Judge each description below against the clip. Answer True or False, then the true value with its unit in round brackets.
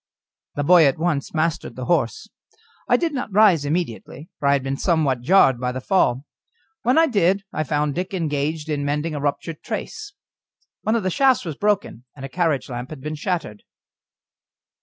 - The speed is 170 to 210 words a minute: True (185 wpm)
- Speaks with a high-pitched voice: False (155 Hz)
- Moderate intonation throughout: True (5.0 semitones)